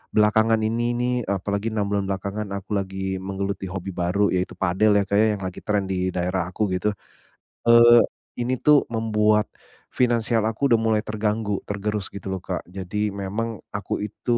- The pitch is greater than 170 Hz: No, low, 105 Hz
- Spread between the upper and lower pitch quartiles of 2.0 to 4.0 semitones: Yes, narrow, 2.4 semitones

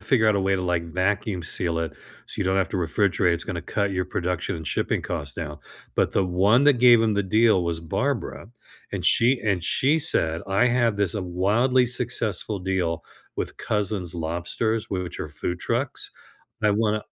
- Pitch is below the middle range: Yes, very low, 95 Hz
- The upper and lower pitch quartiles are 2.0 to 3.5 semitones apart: No, average, 3.9 semitones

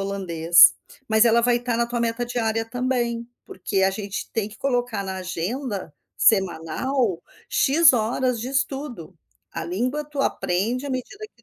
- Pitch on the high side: Yes, high, 235 Hz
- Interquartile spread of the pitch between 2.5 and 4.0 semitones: No, average, 4.4 semitones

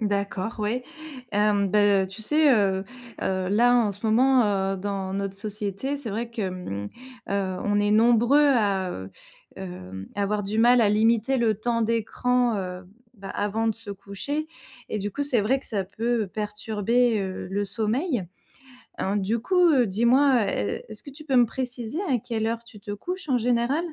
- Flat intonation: No, average, 3.3 semitones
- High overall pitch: Yes, high, 215 Hz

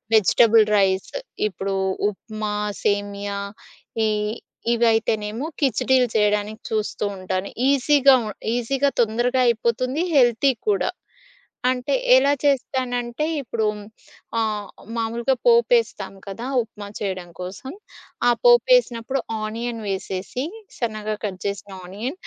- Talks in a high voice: Yes, high, 230 Hz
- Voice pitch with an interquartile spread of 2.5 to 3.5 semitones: No, average, 4.0 semitones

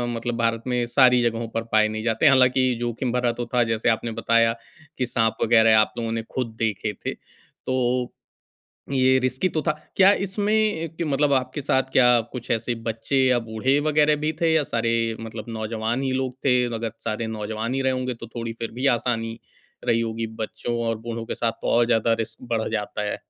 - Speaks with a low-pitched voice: Yes, low, 120 Hz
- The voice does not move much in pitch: Yes, narrow, 2.3 semitones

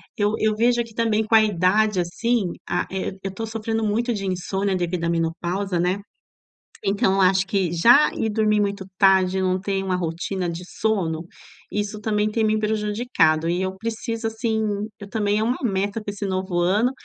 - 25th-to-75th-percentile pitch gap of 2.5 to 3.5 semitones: Yes, average, 2.9 semitones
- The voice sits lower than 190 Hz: No, high, 200 Hz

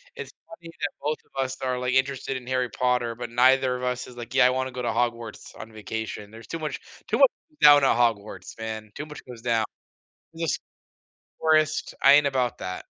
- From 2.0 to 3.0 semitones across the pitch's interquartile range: Yes, average, 2.7 semitones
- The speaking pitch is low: Yes, low, 125 Hz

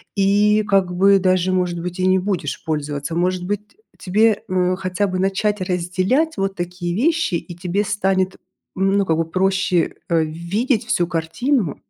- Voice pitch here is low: No, medium, 185 Hz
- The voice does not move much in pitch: Yes, narrow, 2.3 semitones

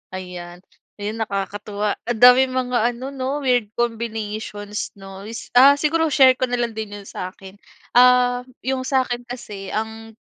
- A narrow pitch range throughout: No, average, 3.7 semitones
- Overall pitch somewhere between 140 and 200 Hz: No, high, 230 Hz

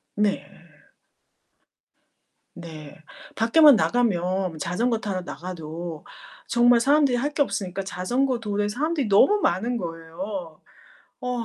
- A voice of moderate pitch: No, high, 205 Hz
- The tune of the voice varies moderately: No, wide, 5.8 semitones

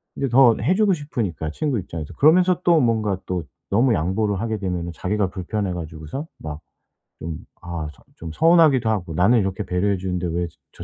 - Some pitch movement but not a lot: No, wide, 6.1 semitones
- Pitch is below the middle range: Yes, low, 100 Hz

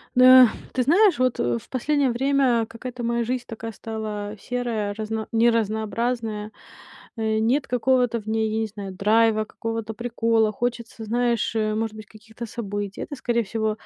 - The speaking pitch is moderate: No, high, 225 Hz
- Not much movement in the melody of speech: Yes, narrow, 2.0 semitones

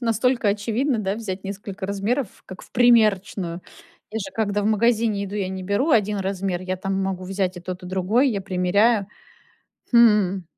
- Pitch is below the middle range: No, high, 200 Hz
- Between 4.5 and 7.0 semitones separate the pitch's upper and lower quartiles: No, average, 2.9 semitones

